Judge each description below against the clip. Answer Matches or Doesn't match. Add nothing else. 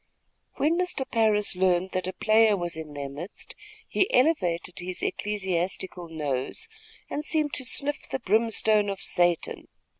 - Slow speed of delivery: Doesn't match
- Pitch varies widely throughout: Doesn't match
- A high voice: Matches